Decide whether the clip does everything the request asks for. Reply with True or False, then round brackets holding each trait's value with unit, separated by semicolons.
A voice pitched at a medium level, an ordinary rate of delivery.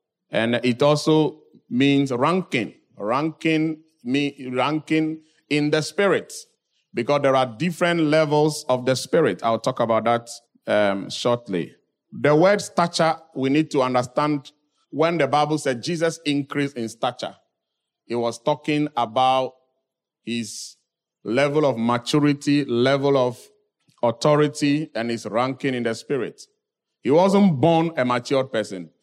False (145 Hz; 130 wpm)